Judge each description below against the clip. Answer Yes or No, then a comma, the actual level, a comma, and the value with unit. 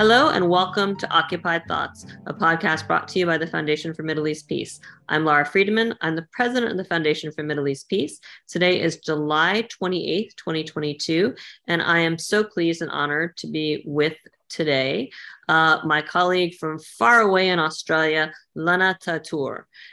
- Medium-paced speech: Yes, average, 170 wpm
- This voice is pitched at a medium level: Yes, medium, 165 Hz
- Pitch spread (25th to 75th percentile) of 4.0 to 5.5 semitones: No, average, 2.8 semitones